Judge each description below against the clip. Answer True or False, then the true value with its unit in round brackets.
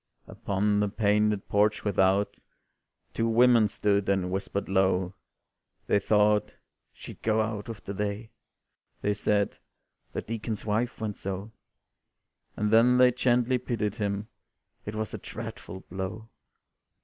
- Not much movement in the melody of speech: True (1.9 semitones)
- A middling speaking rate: False (130 wpm)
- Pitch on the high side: False (105 Hz)